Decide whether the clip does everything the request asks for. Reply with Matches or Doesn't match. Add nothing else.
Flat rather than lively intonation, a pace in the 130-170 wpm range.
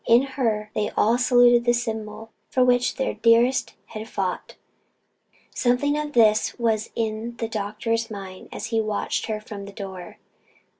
Matches